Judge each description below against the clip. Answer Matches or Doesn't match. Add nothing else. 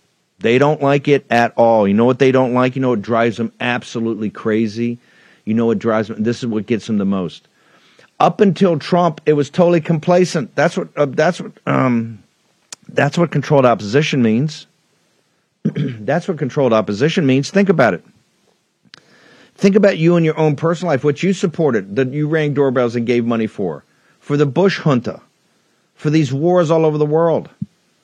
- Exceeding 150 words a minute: Matches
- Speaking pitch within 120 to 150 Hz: Matches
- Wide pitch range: Matches